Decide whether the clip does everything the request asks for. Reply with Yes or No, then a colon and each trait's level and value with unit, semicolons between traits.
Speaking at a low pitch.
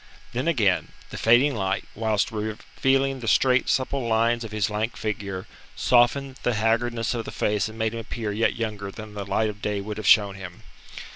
Yes: low, 110 Hz